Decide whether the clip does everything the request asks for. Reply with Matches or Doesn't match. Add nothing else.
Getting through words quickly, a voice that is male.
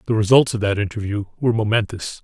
Doesn't match